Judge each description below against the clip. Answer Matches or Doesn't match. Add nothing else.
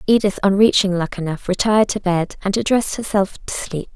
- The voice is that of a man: Doesn't match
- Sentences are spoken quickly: Doesn't match